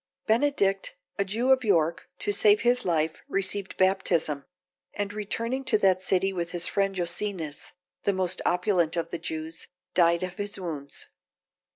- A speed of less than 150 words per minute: No, average, 155 wpm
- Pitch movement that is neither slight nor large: Yes, average, 3.2 semitones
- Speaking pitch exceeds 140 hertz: Yes, high, 190 Hz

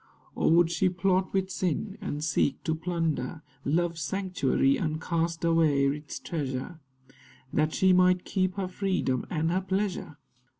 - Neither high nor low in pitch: Yes, medium, 170 Hz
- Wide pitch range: No, average, 3.2 semitones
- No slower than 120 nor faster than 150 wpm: Yes, average, 145 wpm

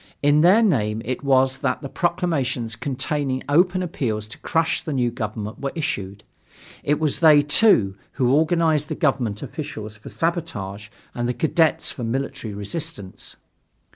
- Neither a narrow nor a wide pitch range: No, wide, 6.2 semitones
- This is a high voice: No, low, 135 Hz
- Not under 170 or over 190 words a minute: No, average, 150 wpm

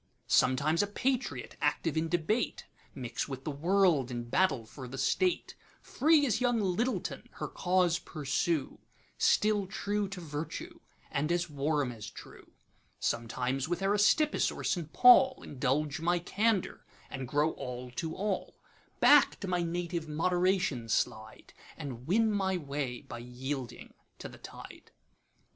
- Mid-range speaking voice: Yes, medium, 165 Hz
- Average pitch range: No, wide, 6.5 semitones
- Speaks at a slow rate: Yes, slow, 125 wpm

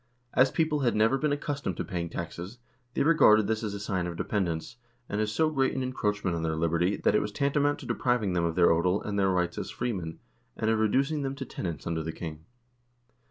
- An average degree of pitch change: No, wide, 7.3 semitones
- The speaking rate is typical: No, fast, 235 wpm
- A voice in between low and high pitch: No, low, 105 Hz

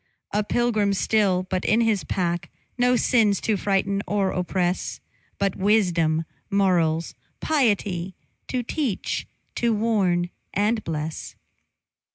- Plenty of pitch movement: No, average, 3.5 semitones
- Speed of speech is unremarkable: No, slow, 115 wpm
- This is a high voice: Yes, high, 200 Hz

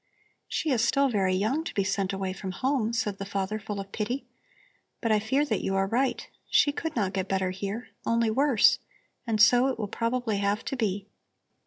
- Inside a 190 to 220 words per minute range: Yes, fast, 205 wpm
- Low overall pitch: No, high, 215 Hz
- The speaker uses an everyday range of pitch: Yes, average, 4.0 semitones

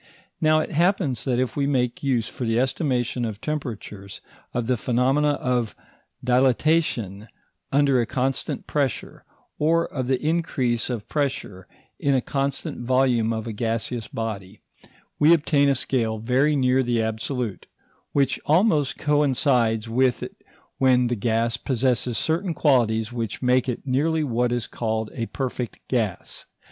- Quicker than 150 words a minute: No, average, 145 wpm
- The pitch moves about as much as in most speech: Yes, average, 3.5 semitones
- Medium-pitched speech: No, low, 125 Hz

